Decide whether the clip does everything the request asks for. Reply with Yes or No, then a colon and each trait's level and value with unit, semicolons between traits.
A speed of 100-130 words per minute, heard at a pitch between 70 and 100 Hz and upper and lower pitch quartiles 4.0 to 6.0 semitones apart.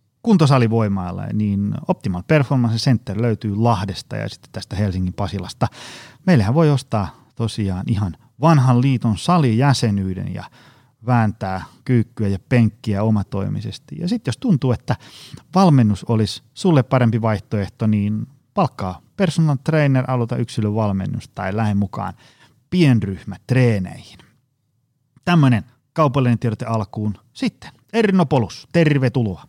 No: average, 110 wpm; low, 120 Hz; average, 4.4 semitones